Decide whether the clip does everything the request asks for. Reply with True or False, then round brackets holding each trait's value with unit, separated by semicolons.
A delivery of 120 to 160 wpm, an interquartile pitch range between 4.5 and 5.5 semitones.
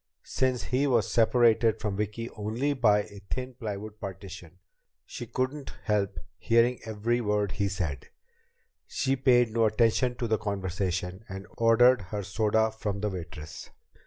False (145 wpm; 3.2 semitones)